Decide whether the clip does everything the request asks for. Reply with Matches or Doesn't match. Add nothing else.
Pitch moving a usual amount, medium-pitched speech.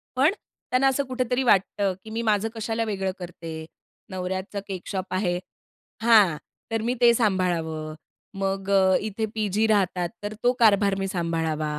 Doesn't match